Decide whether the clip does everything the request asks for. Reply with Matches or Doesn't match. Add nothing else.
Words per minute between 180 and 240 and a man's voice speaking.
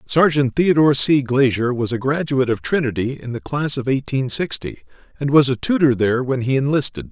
Matches